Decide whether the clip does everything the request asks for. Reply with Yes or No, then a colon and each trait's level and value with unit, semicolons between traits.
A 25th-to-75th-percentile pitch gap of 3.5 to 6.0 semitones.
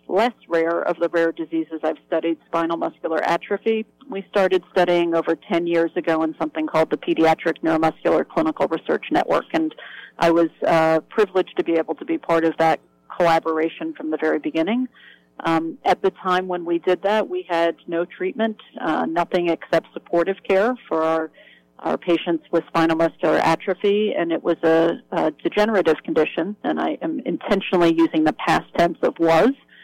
No: narrow, 2.5 semitones